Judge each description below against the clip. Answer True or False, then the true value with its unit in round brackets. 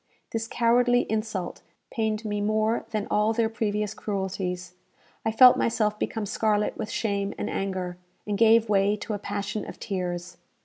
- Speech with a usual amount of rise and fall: False (2.0 semitones)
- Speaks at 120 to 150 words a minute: False (160 wpm)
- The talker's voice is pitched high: True (210 Hz)